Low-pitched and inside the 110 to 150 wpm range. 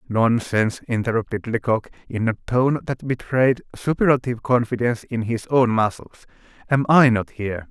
Yes: low, 120 Hz; average, 140 wpm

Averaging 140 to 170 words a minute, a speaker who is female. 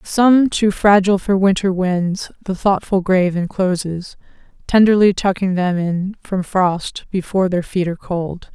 Yes: average, 150 wpm; female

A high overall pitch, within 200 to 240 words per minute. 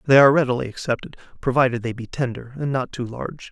No: low, 130 Hz; fast, 205 wpm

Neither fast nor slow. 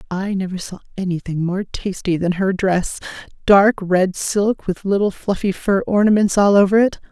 Yes: average, 160 wpm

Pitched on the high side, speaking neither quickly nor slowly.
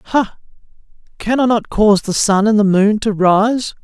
Yes: high, 215 Hz; average, 190 wpm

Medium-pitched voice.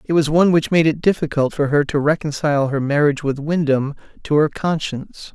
Yes: medium, 150 Hz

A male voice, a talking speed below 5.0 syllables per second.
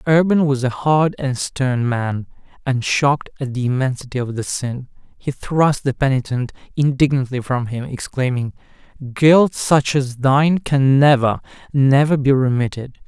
Yes: male; 4.5 syllables/s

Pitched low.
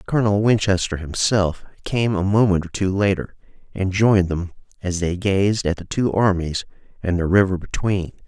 Yes: very low, 95 Hz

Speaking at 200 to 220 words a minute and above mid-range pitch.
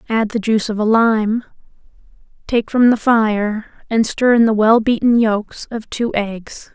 No: average, 180 wpm; high, 220 Hz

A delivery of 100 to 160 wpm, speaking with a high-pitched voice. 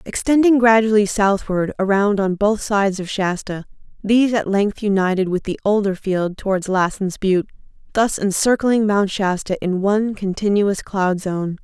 Yes: average, 150 wpm; high, 200 Hz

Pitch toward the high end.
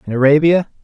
No: medium, 150 Hz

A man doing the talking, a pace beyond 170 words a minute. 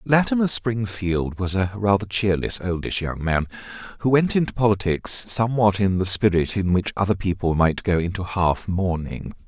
No: male; average, 165 wpm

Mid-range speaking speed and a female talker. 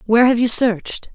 No: fast, 210 wpm; female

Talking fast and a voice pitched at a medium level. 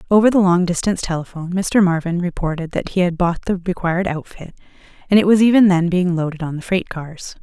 Yes: fast, 210 wpm; medium, 180 Hz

